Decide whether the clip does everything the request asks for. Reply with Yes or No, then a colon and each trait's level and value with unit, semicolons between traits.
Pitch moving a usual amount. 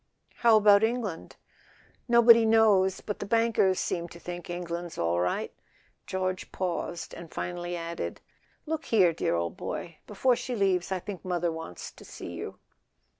Yes: average, 4.3 semitones